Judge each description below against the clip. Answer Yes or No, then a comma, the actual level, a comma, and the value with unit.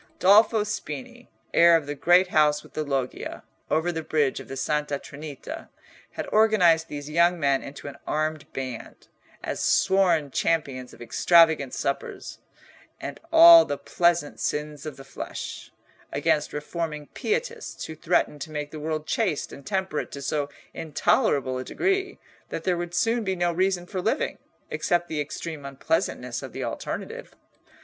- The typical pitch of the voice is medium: Yes, medium, 160 Hz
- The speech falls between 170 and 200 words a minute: No, average, 155 wpm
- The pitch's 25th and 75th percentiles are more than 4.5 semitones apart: No, average, 3.9 semitones